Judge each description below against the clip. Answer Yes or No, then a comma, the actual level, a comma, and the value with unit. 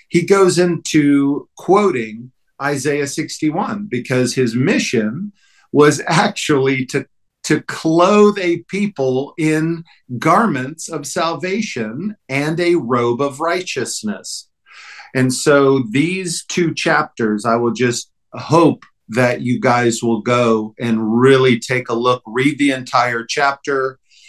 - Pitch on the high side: No, medium, 140 Hz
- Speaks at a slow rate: Yes, slow, 120 wpm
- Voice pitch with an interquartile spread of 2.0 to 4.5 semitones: No, average, 5.2 semitones